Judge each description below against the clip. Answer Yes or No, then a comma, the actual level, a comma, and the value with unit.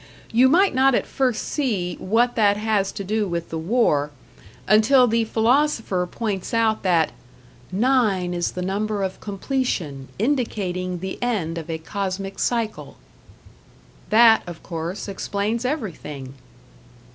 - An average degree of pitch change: Yes, average, 4.6 semitones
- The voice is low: No, high, 205 Hz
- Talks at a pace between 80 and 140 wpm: Yes, slow, 135 wpm